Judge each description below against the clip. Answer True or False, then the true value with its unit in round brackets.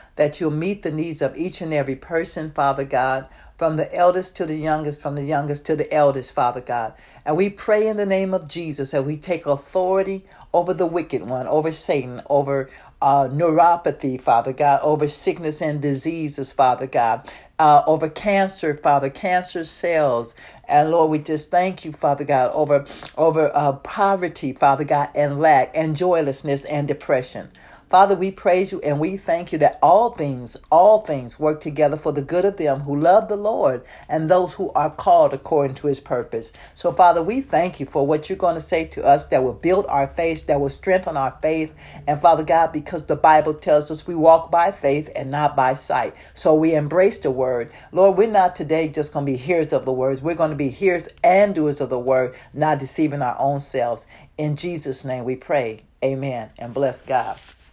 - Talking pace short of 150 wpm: False (200 wpm)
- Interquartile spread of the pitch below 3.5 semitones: False (3.8 semitones)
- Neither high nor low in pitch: True (155 Hz)